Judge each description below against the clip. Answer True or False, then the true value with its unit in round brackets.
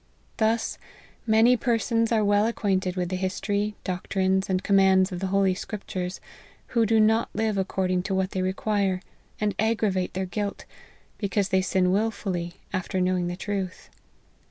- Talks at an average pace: True (155 wpm)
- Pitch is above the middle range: True (195 Hz)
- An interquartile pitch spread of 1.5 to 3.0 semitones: True (2.5 semitones)